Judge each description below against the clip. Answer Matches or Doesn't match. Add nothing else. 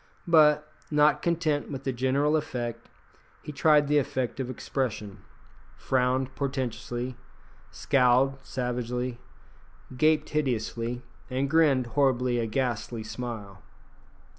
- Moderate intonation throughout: Matches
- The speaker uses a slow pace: Matches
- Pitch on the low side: Matches